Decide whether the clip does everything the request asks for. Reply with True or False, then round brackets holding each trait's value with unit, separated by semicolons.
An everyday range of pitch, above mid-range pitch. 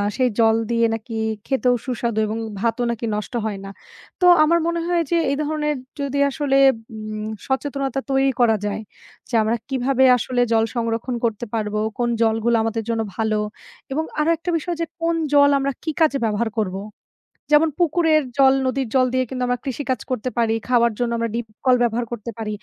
True (3.6 semitones; 245 Hz)